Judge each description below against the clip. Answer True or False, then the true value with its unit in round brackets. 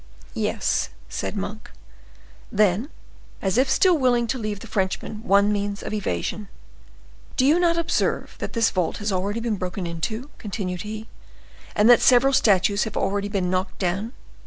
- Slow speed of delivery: False (160 wpm)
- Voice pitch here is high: True (210 Hz)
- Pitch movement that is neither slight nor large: True (3.7 semitones)